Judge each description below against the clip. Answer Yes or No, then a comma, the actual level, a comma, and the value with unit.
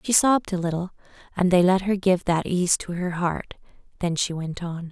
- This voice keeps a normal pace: No, fast, 220 wpm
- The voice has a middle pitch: Yes, medium, 180 Hz